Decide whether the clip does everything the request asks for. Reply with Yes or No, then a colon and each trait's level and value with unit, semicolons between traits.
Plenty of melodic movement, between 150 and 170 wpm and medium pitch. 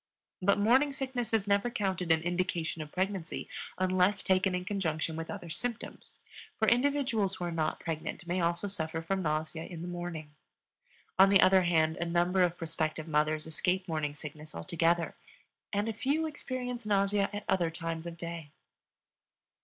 No: average, 3.7 semitones; average, 165 wpm; medium, 180 Hz